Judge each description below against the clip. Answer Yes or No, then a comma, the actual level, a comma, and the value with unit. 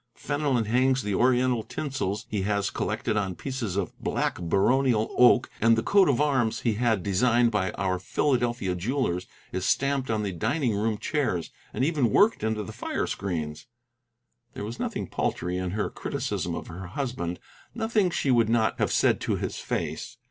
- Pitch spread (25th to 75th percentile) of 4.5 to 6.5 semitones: Yes, average, 5.0 semitones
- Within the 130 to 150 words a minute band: No, average, 175 wpm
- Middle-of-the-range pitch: No, low, 115 Hz